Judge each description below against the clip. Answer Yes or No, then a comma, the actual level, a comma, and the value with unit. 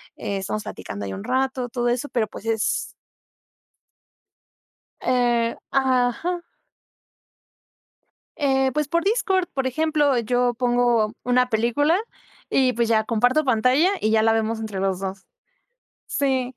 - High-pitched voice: Yes, high, 245 Hz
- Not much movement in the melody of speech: No, average, 3.3 semitones